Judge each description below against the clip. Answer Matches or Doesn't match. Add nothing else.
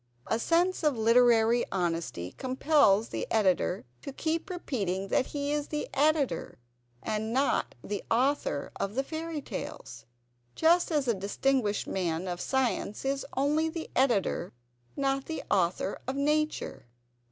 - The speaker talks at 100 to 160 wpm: Matches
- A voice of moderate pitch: Doesn't match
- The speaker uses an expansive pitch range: Matches